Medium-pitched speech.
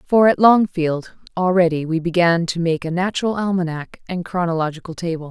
Yes: medium, 175 Hz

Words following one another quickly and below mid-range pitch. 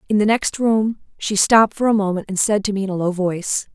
No: fast, 275 wpm; high, 205 Hz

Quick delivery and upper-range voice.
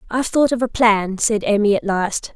Yes: fast, 230 wpm; high, 220 Hz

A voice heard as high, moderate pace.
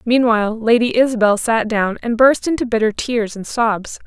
Yes: high, 230 Hz; average, 175 wpm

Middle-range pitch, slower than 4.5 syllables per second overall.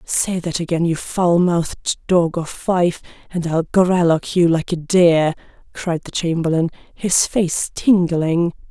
Yes: medium, 170 Hz; 3.9 syllables/s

